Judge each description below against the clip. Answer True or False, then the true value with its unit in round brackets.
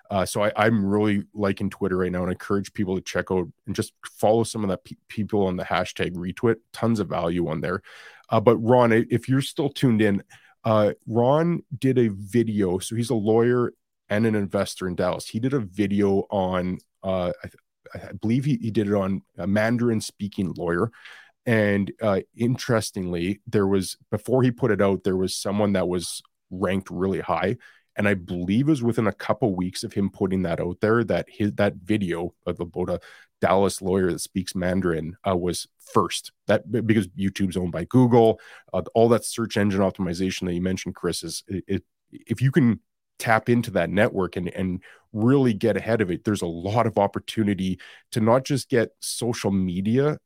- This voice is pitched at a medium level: False (100 Hz)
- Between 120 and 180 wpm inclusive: False (200 wpm)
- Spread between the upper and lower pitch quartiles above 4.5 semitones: False (3.6 semitones)